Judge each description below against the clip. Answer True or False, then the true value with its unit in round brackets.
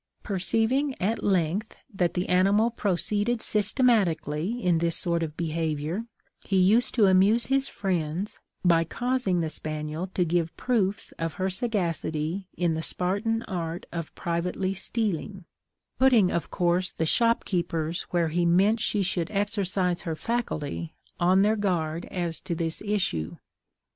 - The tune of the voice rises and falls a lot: False (3.9 semitones)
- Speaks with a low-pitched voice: False (185 Hz)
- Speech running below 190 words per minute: True (140 wpm)